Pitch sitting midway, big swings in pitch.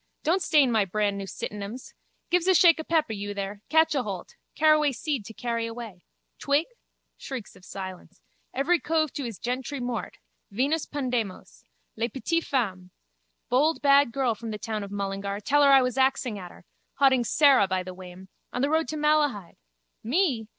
No: high, 245 Hz; wide, 6.1 semitones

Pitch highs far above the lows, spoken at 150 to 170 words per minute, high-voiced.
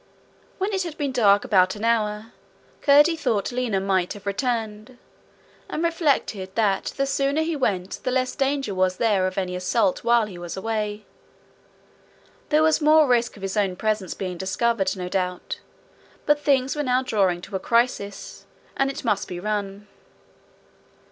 Yes: wide, 5.7 semitones; average, 165 wpm; high, 215 Hz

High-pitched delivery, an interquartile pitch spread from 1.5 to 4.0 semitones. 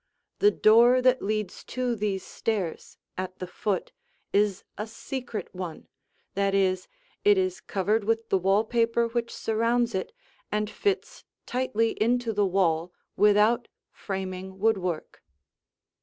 Yes: high, 210 Hz; average, 3.6 semitones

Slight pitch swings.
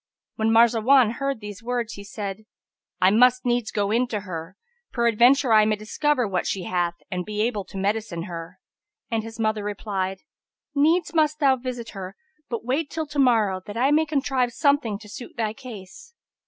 No: average, 3.9 semitones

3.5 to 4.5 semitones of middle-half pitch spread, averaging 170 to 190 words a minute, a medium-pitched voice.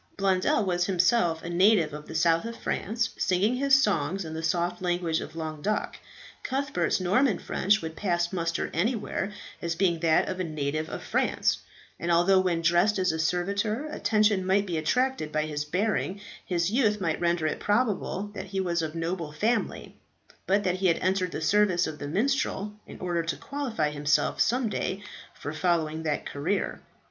Yes: average, 4.0 semitones; average, 180 wpm; medium, 180 Hz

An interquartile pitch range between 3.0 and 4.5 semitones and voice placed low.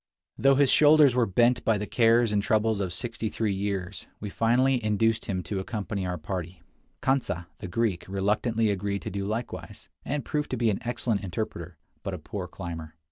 Yes: average, 3.7 semitones; low, 105 Hz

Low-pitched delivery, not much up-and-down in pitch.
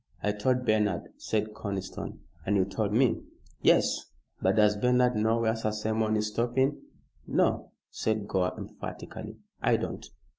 Yes: low, 110 Hz; narrow, 1.9 semitones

